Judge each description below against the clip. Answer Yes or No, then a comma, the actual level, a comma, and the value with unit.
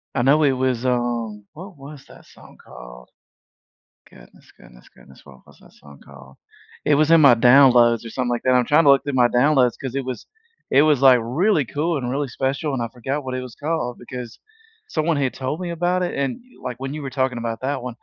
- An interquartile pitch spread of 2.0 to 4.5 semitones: Yes, average, 3.3 semitones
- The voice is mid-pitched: No, low, 130 Hz